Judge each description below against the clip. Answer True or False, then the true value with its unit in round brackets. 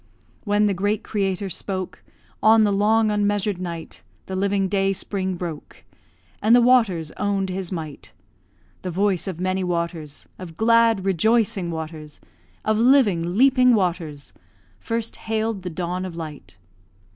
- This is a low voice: False (195 Hz)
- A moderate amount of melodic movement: True (3.6 semitones)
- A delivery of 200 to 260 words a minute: False (140 wpm)